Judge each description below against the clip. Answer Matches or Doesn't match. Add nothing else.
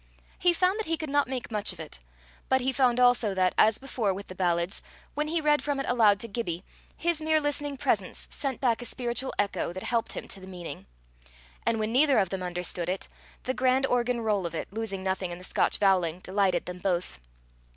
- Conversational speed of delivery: Doesn't match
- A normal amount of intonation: Doesn't match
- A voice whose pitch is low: Doesn't match